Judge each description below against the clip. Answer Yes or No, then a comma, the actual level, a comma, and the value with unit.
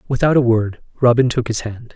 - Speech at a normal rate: No, fast, 215 wpm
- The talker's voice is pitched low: Yes, low, 120 Hz